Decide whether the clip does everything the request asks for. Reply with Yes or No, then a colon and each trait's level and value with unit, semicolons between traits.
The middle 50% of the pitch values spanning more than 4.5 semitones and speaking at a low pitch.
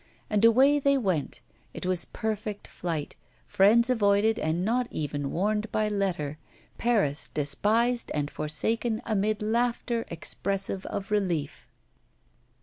No: average, 5.2 semitones; high, 205 Hz